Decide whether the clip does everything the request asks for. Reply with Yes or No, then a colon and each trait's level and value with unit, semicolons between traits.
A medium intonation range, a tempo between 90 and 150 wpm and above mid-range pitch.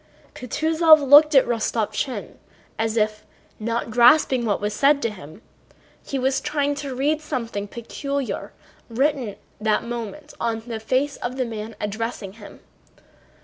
Yes: average, 4.2 semitones; average, 145 wpm; high, 240 Hz